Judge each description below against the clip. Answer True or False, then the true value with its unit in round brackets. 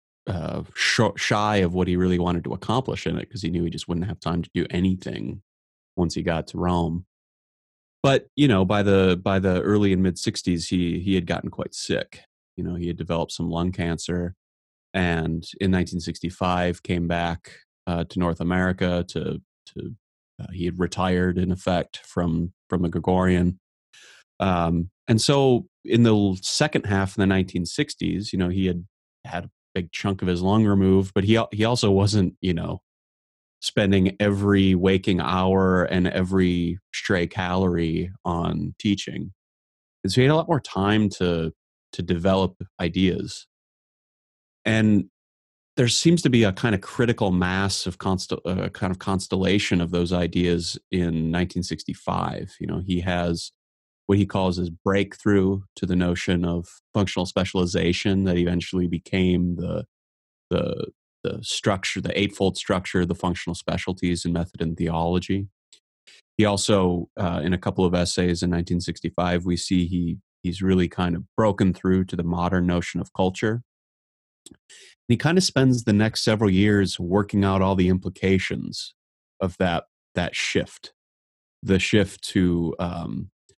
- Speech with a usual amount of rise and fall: False (2.2 semitones)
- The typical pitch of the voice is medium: False (90 Hz)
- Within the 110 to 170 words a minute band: True (160 wpm)